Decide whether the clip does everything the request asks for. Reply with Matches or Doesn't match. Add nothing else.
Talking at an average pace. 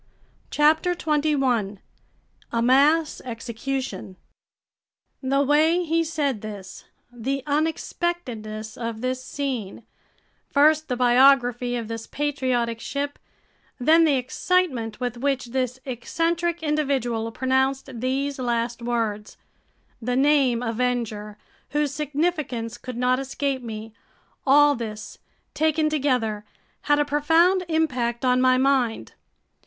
Doesn't match